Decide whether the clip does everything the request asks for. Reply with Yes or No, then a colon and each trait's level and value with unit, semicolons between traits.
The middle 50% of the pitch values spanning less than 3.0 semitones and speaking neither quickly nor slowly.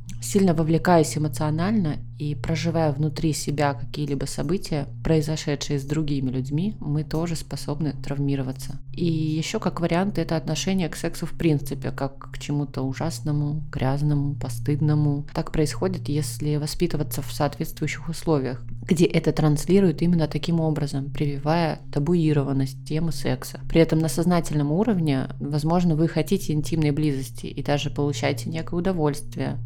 Yes: narrow, 2.5 semitones; average, 130 wpm